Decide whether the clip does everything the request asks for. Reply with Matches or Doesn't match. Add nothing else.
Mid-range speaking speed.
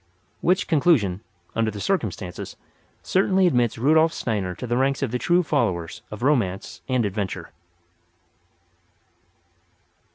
Doesn't match